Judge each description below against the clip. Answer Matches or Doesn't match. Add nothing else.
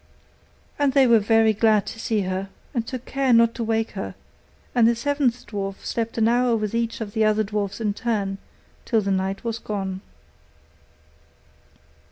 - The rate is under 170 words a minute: Doesn't match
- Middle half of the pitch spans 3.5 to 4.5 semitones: Doesn't match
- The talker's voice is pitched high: Matches